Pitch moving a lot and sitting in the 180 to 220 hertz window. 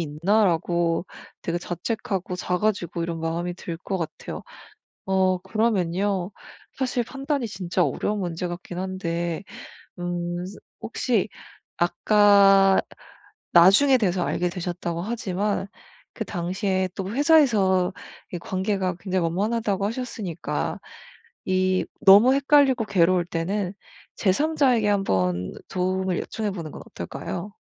No: average, 3.2 semitones; high, 190 Hz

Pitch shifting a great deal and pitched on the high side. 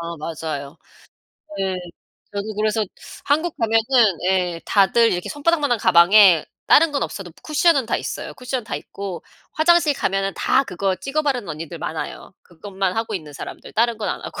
Yes: wide, 6.5 semitones; high, 205 Hz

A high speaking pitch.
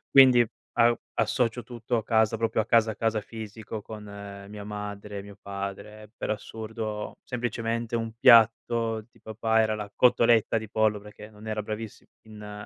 No: low, 110 Hz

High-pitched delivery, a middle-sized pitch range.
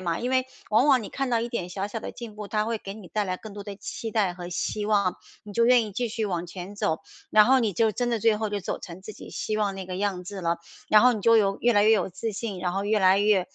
Yes: high, 210 Hz; average, 3.0 semitones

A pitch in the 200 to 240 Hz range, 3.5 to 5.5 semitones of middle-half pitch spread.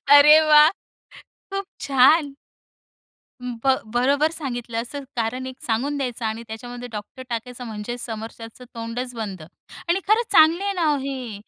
No: very high, 250 Hz; average, 4.1 semitones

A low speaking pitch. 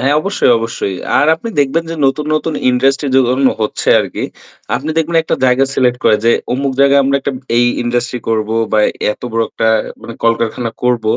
Yes: low, 130 Hz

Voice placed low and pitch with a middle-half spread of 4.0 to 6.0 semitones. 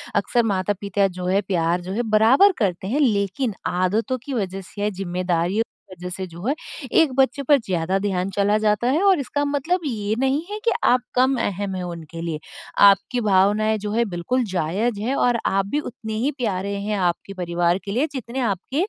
No: high, 205 Hz; average, 5.0 semitones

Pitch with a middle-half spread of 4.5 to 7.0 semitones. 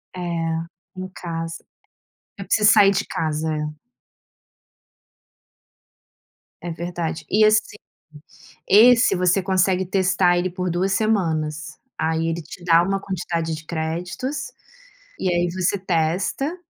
No: average, 2.9 semitones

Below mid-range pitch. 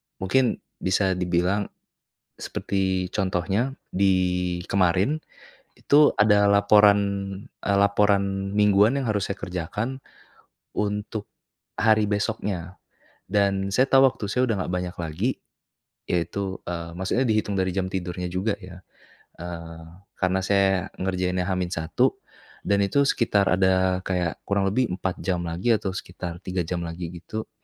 Yes: very low, 95 Hz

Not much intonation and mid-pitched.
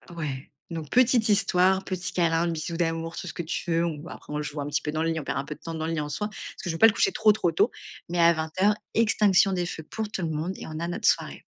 No: average, 3.2 semitones; medium, 165 Hz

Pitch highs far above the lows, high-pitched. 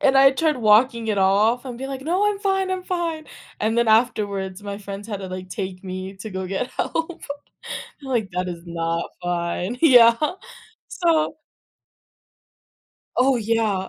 Yes: wide, 6.0 semitones; high, 225 Hz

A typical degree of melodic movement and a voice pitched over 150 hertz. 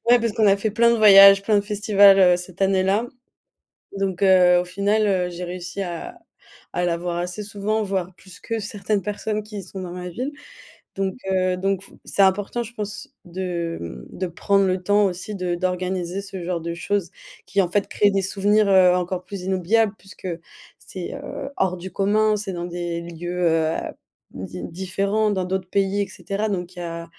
No: narrow, 2.3 semitones; high, 190 Hz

